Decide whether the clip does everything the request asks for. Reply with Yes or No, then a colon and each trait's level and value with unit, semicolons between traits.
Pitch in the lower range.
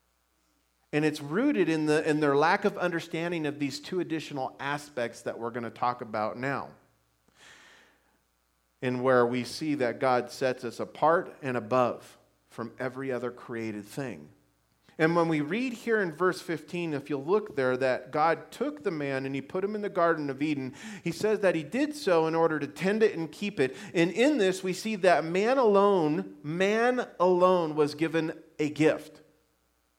No: medium, 150 Hz